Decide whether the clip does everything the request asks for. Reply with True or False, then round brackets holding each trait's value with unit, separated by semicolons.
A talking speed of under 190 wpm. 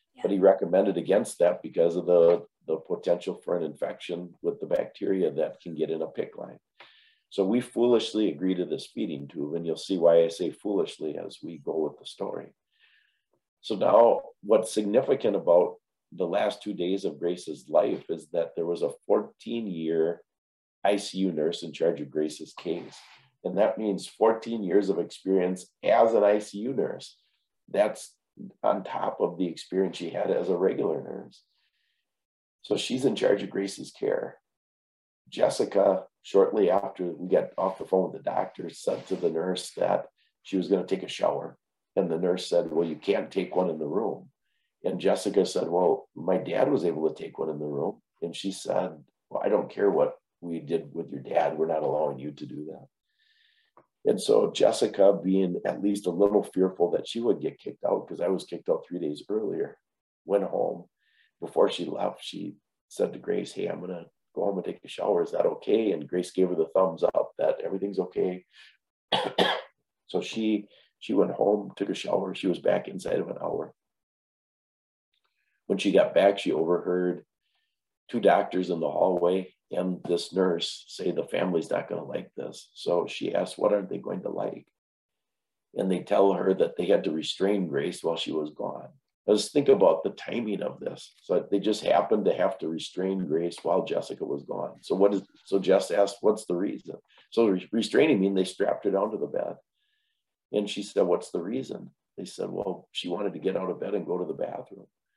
False (195 wpm)